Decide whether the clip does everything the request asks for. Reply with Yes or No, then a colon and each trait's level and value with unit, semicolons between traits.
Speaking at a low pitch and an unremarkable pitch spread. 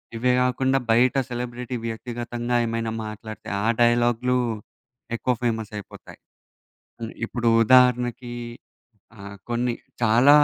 No: low, 120 Hz; narrow, 1.6 semitones